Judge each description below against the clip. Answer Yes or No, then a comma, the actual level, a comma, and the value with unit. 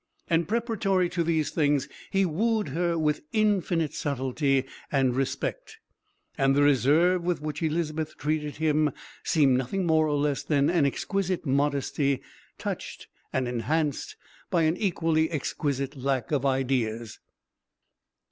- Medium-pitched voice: Yes, medium, 150 Hz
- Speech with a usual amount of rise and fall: Yes, average, 3.7 semitones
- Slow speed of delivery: Yes, slow, 130 wpm